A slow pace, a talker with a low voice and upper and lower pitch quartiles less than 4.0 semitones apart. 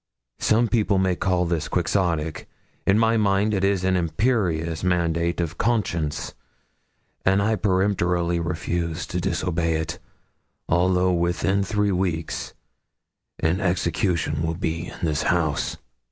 Yes: slow, 125 wpm; very low, 90 Hz; average, 2.7 semitones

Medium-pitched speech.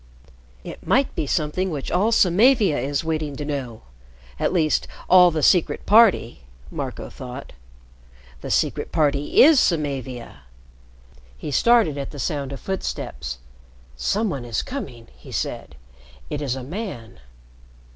Yes: medium, 150 Hz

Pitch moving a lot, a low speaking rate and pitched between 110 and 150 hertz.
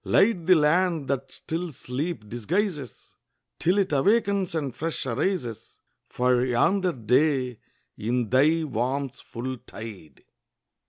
Yes: wide, 6.0 semitones; slow, 115 wpm; medium, 140 Hz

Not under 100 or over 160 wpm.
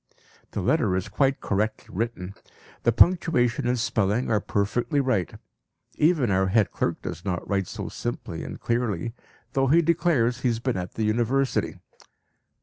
Yes: average, 155 wpm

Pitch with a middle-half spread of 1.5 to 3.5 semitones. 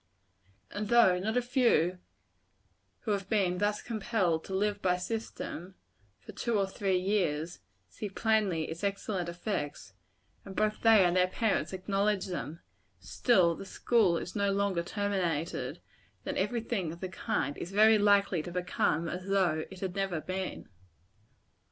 Yes: average, 2.9 semitones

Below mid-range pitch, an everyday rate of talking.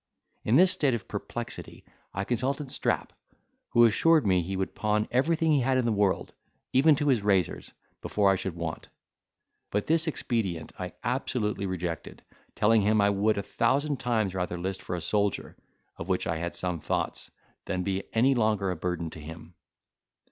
Yes: low, 105 Hz; average, 175 wpm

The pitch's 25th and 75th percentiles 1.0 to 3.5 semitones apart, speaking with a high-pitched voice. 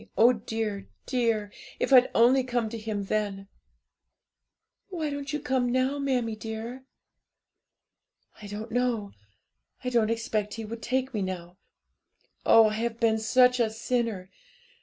Yes: average, 2.8 semitones; high, 230 Hz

